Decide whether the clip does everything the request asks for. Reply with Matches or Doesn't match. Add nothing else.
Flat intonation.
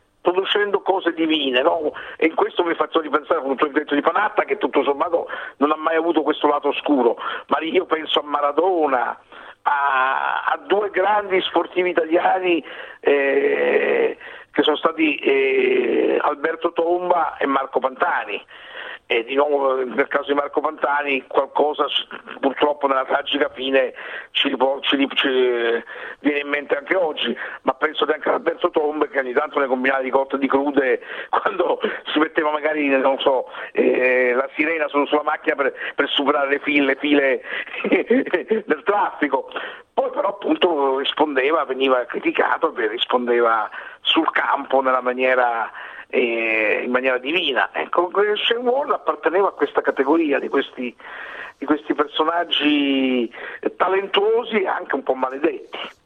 Doesn't match